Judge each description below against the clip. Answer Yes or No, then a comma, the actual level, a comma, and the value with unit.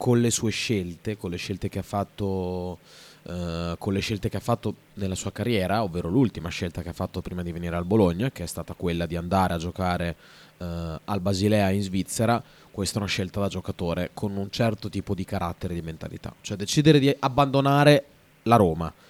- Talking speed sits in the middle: No, fast, 205 wpm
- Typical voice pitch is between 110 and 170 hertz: No, very low, 95 Hz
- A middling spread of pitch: Yes, average, 3.6 semitones